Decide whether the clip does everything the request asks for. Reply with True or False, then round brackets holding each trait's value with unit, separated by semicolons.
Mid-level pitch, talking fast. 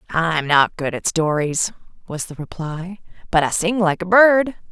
False (175 Hz; 180 wpm)